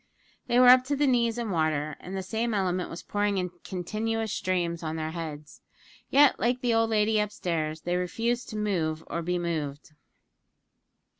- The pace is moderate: Yes, average, 180 wpm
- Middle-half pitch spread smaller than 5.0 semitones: No, average, 5.3 semitones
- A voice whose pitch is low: No, high, 190 Hz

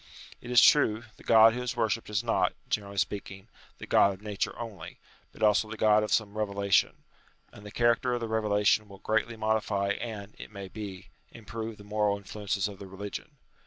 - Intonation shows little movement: Yes, narrow, 1.9 semitones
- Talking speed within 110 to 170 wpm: No, average, 200 wpm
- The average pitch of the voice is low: Yes, low, 105 Hz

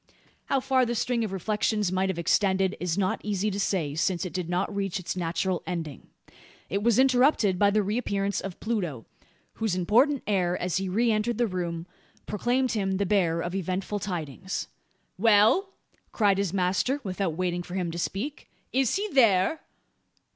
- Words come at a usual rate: Yes, average, 175 wpm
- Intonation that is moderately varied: Yes, average, 3.4 semitones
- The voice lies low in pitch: No, high, 195 Hz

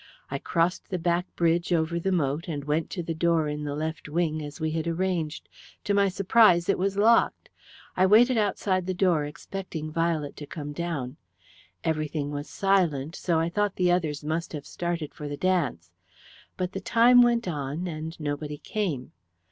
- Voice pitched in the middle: Yes, medium, 165 Hz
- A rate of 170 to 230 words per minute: Yes, average, 180 wpm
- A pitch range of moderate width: Yes, average, 3.7 semitones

